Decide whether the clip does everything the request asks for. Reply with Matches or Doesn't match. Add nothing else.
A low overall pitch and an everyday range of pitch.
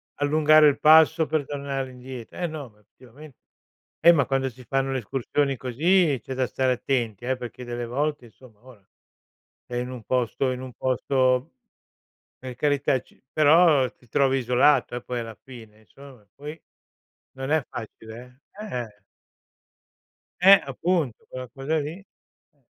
Matches